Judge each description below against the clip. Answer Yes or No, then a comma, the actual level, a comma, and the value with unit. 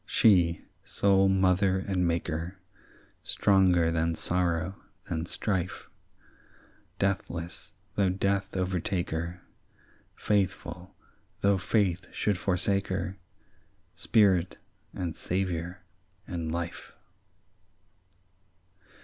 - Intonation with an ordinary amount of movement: No, narrow, 2.2 semitones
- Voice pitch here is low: Yes, very low, 90 Hz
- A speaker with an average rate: No, slow, 80 wpm